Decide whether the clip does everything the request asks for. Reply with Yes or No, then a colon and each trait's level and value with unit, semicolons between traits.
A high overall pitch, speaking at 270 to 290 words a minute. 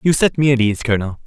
No: low, 125 Hz; fast, 285 wpm